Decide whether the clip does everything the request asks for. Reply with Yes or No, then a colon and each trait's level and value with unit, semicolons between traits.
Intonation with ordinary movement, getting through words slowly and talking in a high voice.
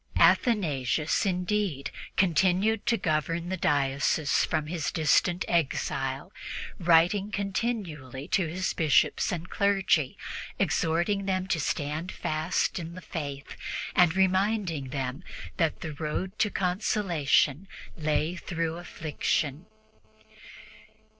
No: average, 3.9 semitones; slow, 105 wpm; medium, 170 Hz